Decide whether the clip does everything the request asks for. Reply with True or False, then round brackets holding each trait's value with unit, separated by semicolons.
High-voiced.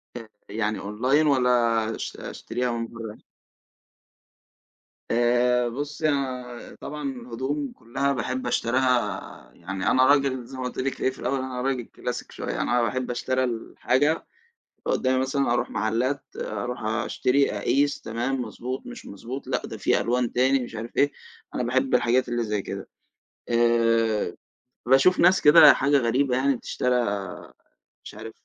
False (125 Hz)